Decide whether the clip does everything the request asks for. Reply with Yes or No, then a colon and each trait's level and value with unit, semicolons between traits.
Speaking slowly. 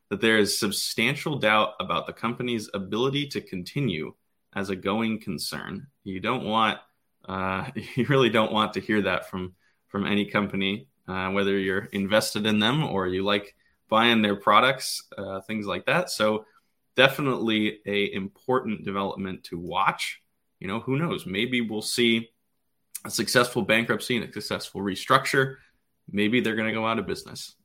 No: average, 165 wpm